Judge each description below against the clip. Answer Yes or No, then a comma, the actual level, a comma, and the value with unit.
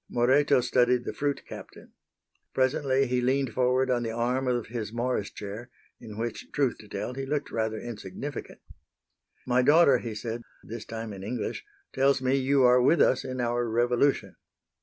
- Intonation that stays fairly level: Yes, narrow, 2.2 semitones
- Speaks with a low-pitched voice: Yes, low, 125 Hz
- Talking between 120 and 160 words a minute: No, average, 170 wpm